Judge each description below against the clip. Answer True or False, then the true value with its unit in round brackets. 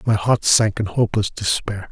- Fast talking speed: False (190 wpm)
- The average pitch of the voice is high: False (105 Hz)